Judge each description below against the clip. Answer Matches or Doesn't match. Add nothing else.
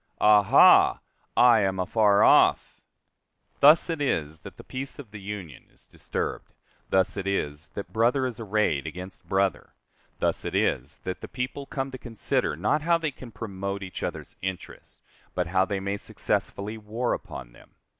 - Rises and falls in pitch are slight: Doesn't match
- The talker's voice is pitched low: Matches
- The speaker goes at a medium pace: Matches